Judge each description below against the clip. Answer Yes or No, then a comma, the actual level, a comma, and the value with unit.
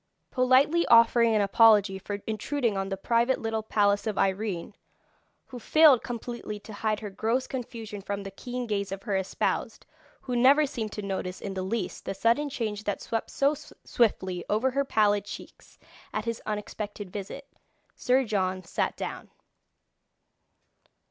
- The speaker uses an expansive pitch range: No, average, 3.4 semitones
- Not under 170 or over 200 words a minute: No, average, 155 wpm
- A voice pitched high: Yes, high, 215 Hz